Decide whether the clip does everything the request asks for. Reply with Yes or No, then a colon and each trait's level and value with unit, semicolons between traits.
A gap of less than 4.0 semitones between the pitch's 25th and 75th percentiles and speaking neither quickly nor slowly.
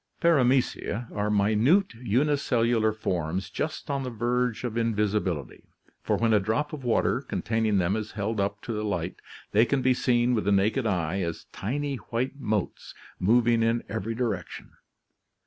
Yes: average, 3.4 semitones; average, 170 wpm